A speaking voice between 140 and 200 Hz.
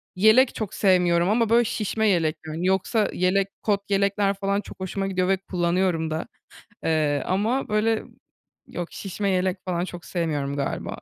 Yes: high, 190 Hz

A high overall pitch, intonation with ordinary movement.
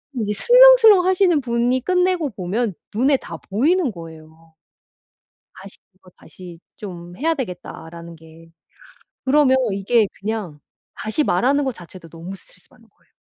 No: high, 215 Hz; wide, 8.8 semitones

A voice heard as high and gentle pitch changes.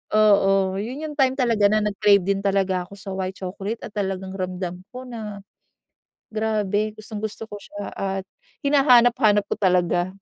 Yes: high, 205 Hz; narrow, 2.2 semitones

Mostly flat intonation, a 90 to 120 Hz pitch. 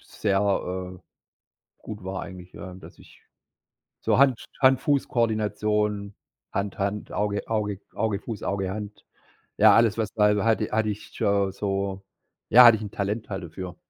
Yes: narrow, 1.8 semitones; low, 105 Hz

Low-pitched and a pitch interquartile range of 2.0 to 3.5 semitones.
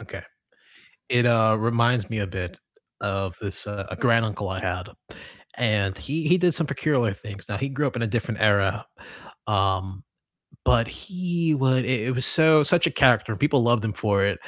No: low, 115 Hz; average, 5.1 semitones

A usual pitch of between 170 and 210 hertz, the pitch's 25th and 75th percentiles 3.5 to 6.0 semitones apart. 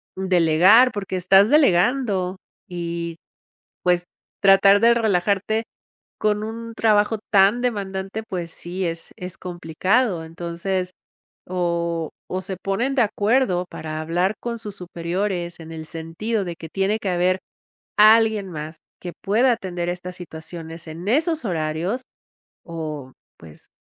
Yes: medium, 185 Hz; average, 3.8 semitones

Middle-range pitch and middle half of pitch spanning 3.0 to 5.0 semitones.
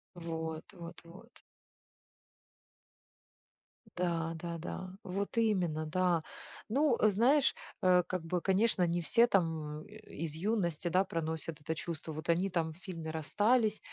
Yes: medium, 175 Hz; average, 3.3 semitones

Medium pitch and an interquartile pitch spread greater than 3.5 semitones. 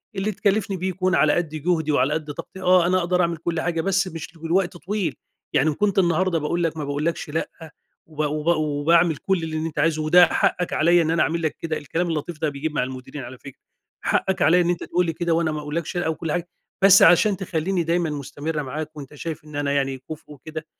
No: medium, 165 Hz; average, 2.7 semitones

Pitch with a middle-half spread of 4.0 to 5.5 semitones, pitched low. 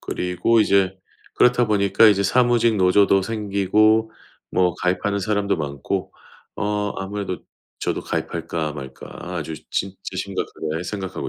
No: average, 2.7 semitones; low, 100 Hz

